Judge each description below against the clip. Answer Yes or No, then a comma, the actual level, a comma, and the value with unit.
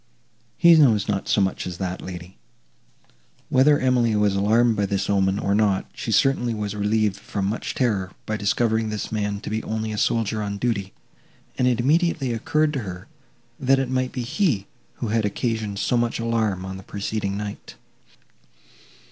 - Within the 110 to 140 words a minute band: No, average, 175 wpm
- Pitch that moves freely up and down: No, average, 3.2 semitones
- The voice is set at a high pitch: No, low, 110 Hz